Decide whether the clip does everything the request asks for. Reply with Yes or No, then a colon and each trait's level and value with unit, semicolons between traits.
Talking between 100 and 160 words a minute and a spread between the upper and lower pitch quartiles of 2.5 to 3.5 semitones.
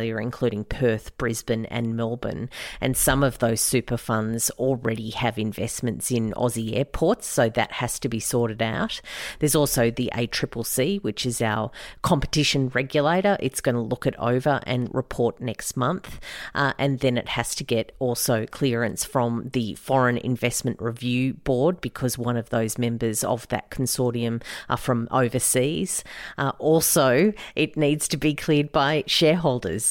Yes: average, 155 wpm; average, 2.9 semitones